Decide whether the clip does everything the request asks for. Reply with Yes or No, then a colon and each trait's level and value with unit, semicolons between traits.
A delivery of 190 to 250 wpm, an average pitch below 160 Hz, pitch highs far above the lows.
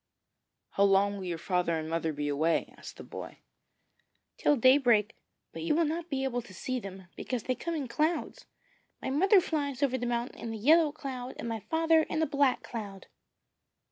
No: average, 195 wpm; very high, 250 Hz; wide, 7.0 semitones